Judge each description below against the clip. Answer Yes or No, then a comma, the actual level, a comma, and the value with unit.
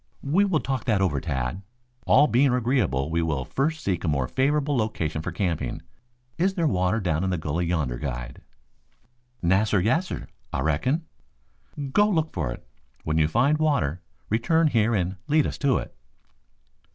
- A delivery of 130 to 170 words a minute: Yes, average, 165 wpm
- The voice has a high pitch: No, low, 100 Hz